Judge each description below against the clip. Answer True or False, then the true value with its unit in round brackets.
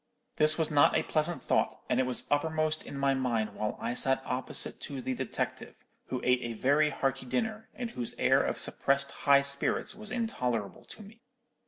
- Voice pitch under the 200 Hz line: True (140 Hz)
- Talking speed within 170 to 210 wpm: True (190 wpm)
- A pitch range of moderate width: True (3.7 semitones)